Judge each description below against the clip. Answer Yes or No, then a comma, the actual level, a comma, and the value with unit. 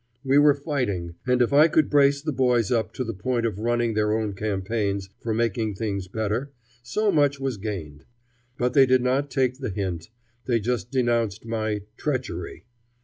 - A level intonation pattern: No, average, 4.0 semitones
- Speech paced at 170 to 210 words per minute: Yes, average, 180 wpm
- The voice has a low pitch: Yes, low, 115 Hz